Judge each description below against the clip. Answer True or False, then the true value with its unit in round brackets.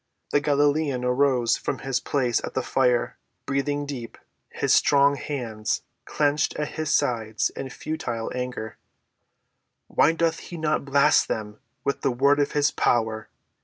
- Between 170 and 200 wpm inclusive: False (145 wpm)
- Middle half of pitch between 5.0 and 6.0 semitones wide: False (3.1 semitones)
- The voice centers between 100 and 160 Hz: True (140 Hz)